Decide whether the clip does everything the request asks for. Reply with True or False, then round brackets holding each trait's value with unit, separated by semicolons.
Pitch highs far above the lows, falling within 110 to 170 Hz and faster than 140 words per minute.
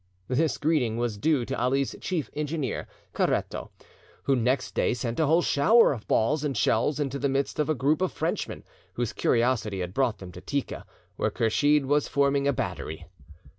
False (4.1 semitones; 135 Hz; 180 wpm)